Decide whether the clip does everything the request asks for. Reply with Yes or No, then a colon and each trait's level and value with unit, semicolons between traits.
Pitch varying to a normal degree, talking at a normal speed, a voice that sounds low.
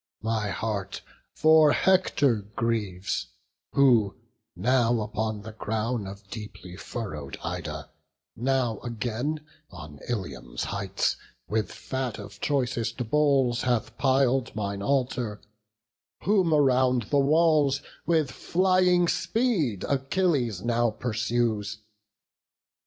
No: average, 4.7 semitones; slow, 100 wpm; low, 120 Hz